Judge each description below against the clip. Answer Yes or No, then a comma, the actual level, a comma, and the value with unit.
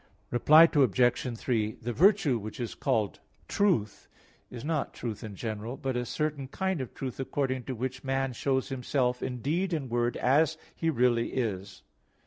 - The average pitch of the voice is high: No, low, 130 Hz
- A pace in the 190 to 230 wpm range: No, average, 165 wpm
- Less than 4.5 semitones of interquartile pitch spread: Yes, average, 3.4 semitones